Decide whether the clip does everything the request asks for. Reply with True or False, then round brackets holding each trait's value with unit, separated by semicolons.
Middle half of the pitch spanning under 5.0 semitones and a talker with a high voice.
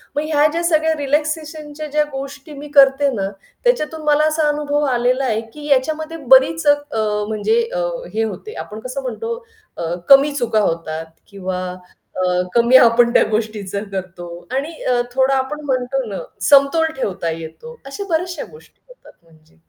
False (5.5 semitones; 275 Hz)